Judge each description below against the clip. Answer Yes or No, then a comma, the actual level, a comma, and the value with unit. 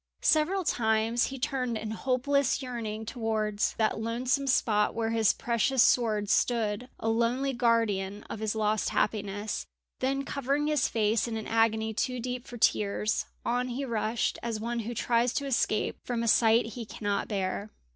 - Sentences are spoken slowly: No, average, 165 wpm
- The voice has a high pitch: Yes, high, 230 Hz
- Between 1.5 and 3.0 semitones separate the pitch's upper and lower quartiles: Yes, narrow, 2.5 semitones